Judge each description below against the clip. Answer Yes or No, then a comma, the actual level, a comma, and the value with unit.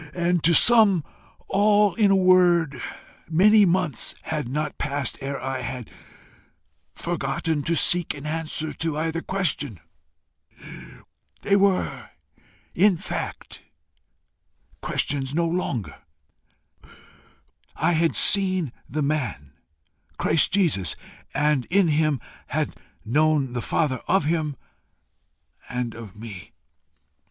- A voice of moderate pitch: Yes, medium, 155 Hz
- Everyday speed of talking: No, slow, 110 wpm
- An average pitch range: Yes, average, 4.8 semitones